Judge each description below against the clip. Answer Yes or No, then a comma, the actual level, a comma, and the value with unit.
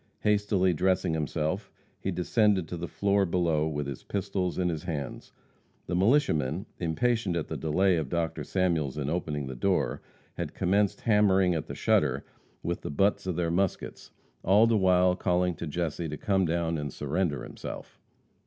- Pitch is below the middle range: Yes, very low, 90 Hz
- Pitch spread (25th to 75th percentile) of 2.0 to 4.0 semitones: Yes, average, 3.4 semitones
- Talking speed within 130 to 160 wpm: No, average, 170 wpm